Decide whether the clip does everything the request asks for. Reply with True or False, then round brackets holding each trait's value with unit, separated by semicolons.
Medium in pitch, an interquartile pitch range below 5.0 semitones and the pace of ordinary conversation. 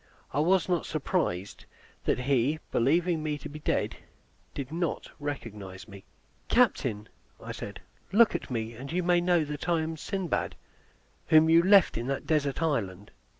False (150 Hz; 5.6 semitones; 160 wpm)